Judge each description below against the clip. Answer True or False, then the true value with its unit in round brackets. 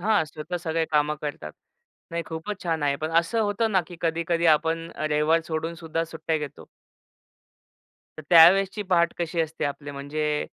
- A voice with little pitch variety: True (1.9 semitones)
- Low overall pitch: False (165 Hz)